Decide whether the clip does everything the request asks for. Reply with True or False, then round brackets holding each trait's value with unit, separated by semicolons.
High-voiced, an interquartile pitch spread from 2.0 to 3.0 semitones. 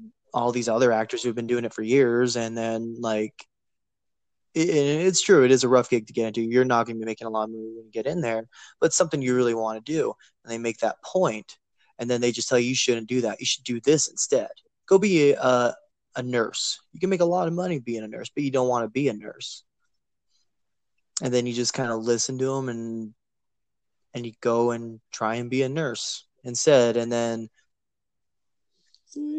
False (120 Hz; 2.6 semitones)